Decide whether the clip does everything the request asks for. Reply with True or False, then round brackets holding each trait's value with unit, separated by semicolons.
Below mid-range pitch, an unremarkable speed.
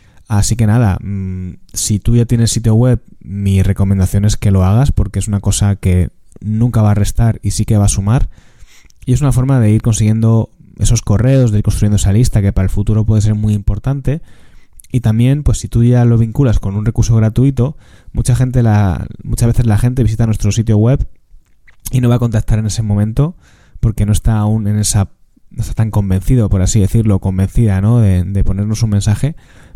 False (110 Hz; 210 wpm)